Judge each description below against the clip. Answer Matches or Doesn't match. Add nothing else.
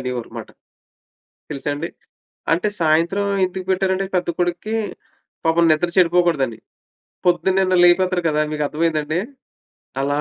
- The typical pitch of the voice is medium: Matches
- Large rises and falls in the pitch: Doesn't match